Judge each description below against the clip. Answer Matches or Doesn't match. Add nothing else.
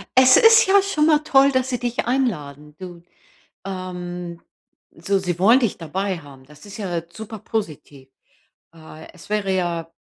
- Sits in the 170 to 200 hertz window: Matches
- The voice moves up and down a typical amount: Doesn't match